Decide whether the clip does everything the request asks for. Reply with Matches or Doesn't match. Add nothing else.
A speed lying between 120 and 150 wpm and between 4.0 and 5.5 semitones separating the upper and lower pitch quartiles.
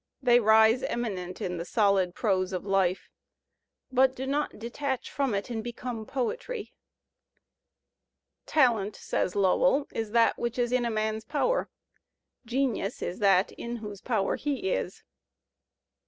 Matches